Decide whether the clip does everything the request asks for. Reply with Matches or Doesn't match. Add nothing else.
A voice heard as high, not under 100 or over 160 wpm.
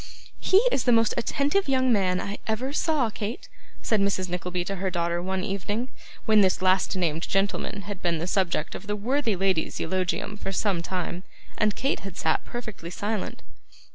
Doesn't match